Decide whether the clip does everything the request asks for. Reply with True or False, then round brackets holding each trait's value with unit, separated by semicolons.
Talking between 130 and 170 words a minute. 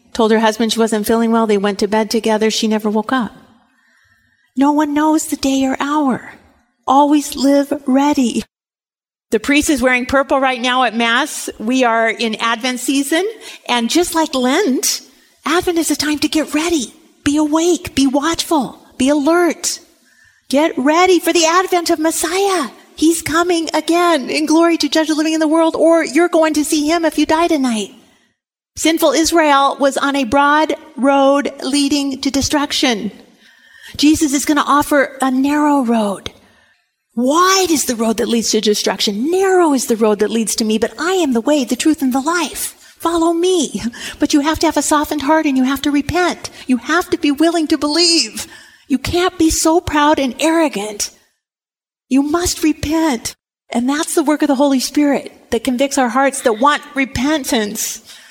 False (180 wpm)